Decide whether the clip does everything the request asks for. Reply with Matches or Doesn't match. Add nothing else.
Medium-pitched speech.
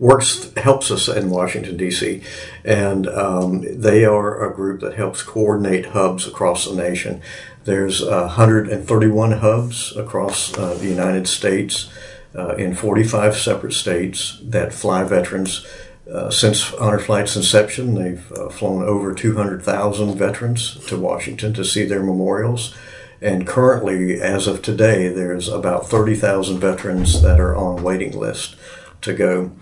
Doesn't match